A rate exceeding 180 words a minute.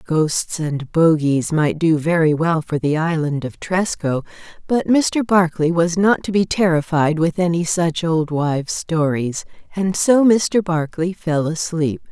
No: average, 160 wpm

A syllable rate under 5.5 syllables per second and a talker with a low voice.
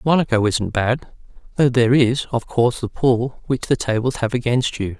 Yes: 5.0 syllables/s; low, 120 Hz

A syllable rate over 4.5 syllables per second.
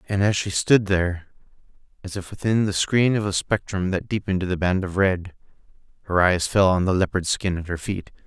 Yes: 5.5 syllables/s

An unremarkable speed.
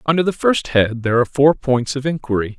No: fast, 230 wpm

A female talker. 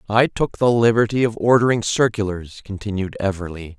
No: male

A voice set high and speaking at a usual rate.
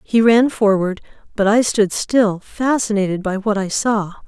Yes: high, 210 Hz; average, 170 wpm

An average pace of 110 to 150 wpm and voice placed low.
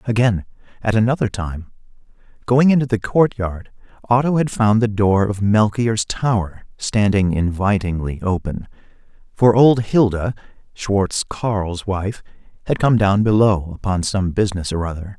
Yes: average, 140 wpm; low, 105 Hz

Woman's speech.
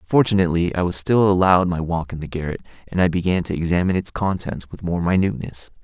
No: male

